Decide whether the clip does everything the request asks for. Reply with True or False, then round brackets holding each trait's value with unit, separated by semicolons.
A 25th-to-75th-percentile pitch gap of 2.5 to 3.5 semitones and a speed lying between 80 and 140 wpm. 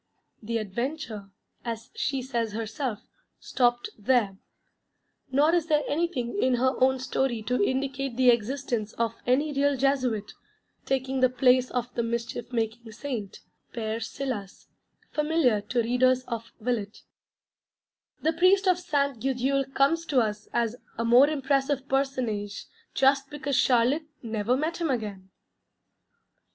True (3.2 semitones; 135 wpm)